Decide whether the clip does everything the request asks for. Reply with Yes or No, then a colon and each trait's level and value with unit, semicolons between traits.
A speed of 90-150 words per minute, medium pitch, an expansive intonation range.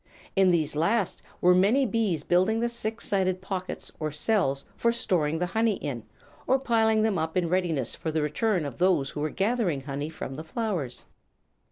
No: average, 185 wpm; medium, 180 Hz; wide, 6.1 semitones